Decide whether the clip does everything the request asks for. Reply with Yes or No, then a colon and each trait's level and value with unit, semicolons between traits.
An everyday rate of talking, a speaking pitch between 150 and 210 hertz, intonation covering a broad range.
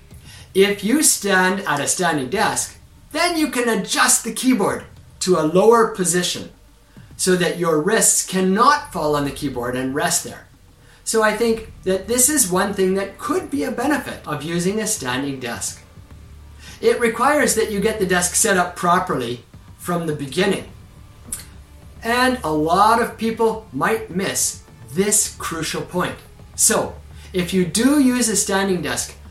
Yes: average, 160 wpm; medium, 185 Hz; wide, 7.4 semitones